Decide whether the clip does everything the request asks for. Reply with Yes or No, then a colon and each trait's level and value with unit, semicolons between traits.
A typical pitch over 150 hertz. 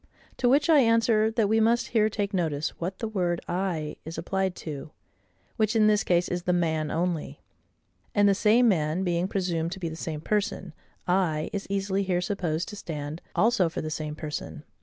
Yes: medium, 185 Hz